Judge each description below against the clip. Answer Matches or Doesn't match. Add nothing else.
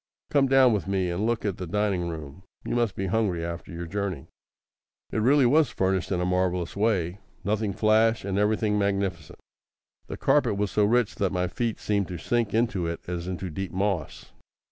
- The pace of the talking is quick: Doesn't match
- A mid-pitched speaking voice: Doesn't match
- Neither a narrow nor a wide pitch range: Matches